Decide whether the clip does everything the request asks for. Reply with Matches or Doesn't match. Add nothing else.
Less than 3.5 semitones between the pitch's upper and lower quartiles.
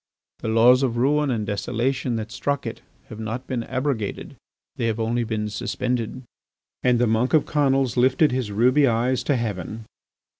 Matches